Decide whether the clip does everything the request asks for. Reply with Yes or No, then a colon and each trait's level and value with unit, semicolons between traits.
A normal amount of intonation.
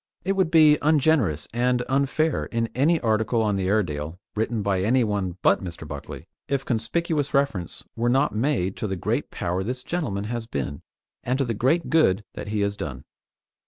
No: wide, 6.2 semitones